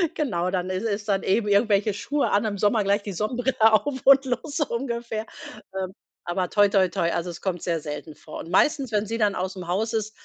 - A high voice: Yes, high, 205 Hz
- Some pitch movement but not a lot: Yes, average, 3.9 semitones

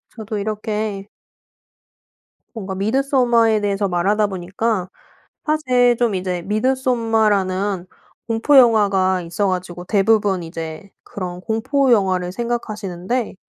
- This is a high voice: Yes, high, 205 Hz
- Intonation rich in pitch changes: No, average, 3.6 semitones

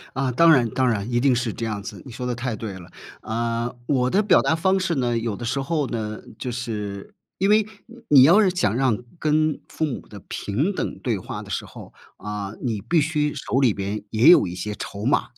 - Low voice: Yes, low, 125 Hz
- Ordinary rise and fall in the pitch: No, wide, 5.9 semitones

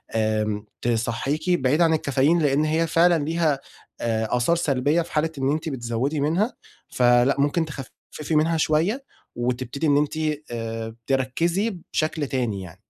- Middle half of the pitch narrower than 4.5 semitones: No, average, 4.9 semitones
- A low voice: No, medium, 145 Hz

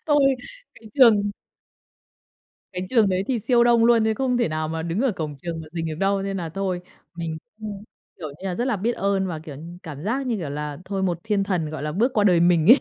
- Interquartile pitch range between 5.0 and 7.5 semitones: Yes, wide, 5.4 semitones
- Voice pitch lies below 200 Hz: Yes, high, 190 Hz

